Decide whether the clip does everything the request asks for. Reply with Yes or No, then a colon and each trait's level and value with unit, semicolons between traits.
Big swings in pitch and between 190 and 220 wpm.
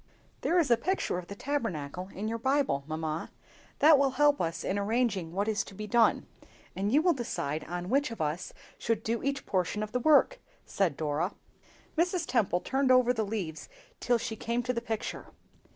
Yes: wide, 6.5 semitones; average, 195 wpm